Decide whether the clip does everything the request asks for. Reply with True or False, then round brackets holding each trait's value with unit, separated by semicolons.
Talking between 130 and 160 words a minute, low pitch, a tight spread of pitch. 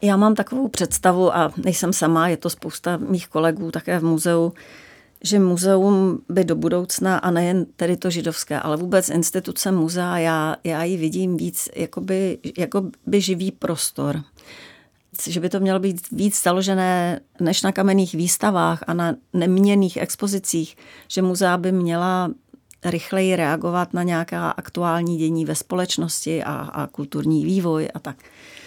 False (150 wpm; 175 Hz; 2.2 semitones)